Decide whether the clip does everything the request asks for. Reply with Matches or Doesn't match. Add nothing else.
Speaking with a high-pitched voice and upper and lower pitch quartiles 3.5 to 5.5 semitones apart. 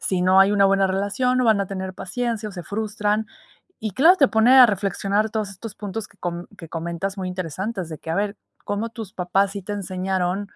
Doesn't match